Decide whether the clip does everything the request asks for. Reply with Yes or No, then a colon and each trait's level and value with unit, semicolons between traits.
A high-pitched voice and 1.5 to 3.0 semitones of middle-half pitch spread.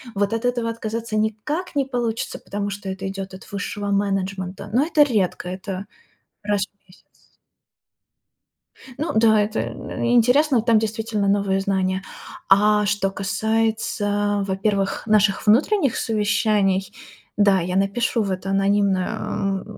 Yes: high, 205 Hz; narrow, 2.4 semitones